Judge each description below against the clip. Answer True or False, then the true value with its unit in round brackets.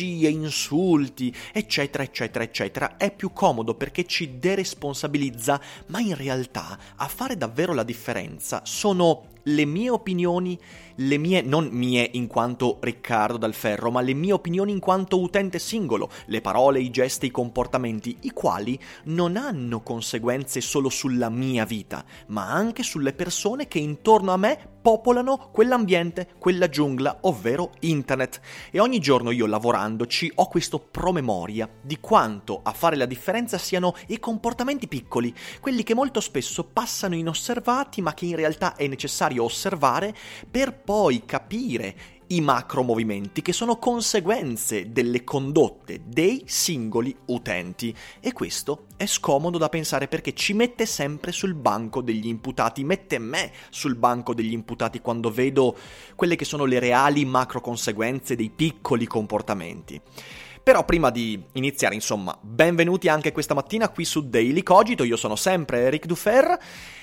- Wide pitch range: True (7.1 semitones)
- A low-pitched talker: False (145 Hz)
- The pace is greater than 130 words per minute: True (145 wpm)